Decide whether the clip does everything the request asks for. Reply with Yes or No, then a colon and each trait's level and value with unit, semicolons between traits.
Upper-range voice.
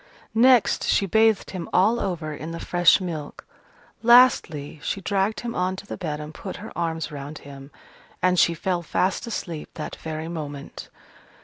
No: medium, 175 Hz